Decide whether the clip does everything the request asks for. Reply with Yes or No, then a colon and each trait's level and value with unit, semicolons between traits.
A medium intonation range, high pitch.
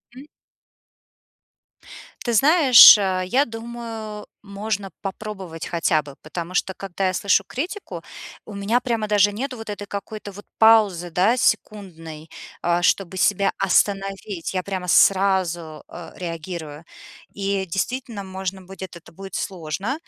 Yes: average, 3.1 semitones; high, 195 Hz